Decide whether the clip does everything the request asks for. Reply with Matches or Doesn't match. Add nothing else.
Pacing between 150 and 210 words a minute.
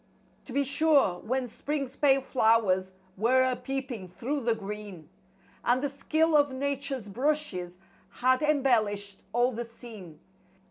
Doesn't match